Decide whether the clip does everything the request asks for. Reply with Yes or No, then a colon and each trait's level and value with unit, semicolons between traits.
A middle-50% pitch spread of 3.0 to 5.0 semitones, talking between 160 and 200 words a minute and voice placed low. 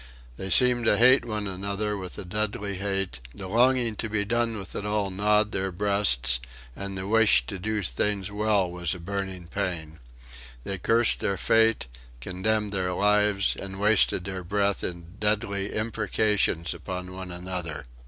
No: narrow, 2.5 semitones; average, 165 wpm; low, 100 Hz